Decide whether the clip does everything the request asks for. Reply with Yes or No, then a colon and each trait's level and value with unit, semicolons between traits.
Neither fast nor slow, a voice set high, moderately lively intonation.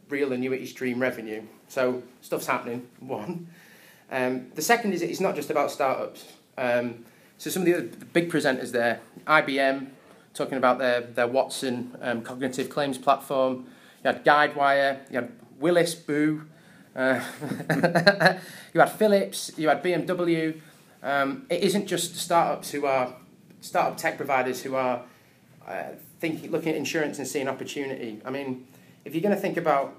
No: average, 155 wpm; medium, 140 Hz; average, 4.6 semitones